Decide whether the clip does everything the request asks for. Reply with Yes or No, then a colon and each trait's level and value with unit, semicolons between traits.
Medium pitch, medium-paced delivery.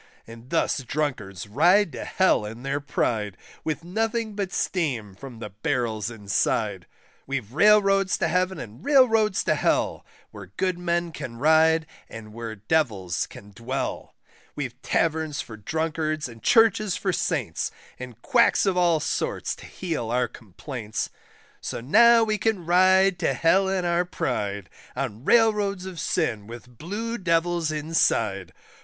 Yes: medium, 155 Hz; average, 145 wpm